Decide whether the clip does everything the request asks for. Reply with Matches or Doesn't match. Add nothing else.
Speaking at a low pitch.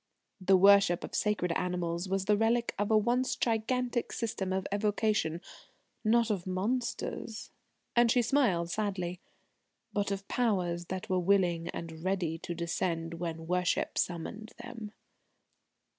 Doesn't match